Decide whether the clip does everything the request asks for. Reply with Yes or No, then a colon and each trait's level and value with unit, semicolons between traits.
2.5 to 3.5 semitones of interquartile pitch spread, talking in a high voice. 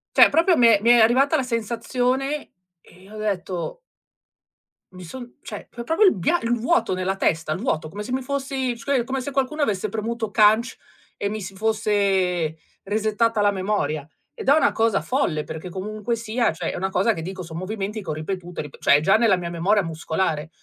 No: average, 4.8 semitones; high, 210 Hz